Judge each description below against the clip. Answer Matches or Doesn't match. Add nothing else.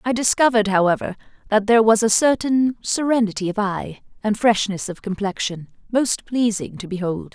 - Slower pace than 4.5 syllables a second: Doesn't match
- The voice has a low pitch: Doesn't match